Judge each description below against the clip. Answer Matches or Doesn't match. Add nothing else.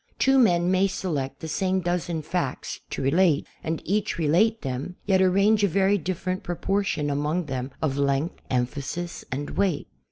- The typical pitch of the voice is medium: Matches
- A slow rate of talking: Doesn't match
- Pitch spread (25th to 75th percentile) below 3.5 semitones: Doesn't match